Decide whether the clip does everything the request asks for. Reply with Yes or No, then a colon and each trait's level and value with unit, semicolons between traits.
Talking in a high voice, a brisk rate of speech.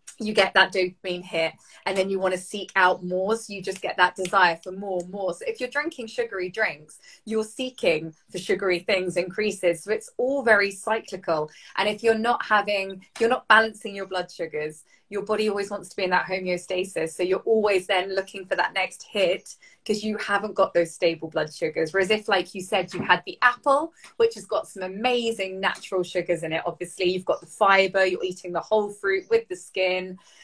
Yes: high, 195 Hz; fast, 215 wpm